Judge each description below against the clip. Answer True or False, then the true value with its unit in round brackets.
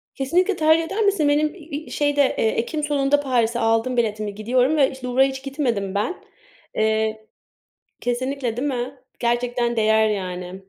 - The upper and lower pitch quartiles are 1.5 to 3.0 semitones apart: False (4.6 semitones)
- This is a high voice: True (250 Hz)